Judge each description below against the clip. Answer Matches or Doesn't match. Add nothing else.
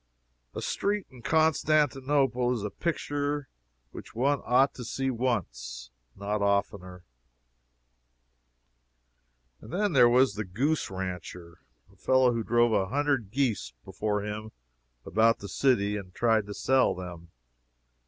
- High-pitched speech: Doesn't match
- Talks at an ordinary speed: Doesn't match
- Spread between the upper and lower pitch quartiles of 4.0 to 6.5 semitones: Matches